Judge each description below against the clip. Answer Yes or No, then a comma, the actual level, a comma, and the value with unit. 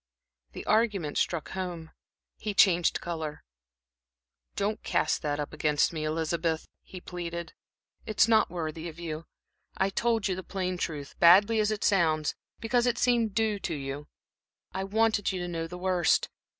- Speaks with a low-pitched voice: No, medium, 175 Hz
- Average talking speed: Yes, average, 160 wpm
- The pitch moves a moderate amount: Yes, average, 4.3 semitones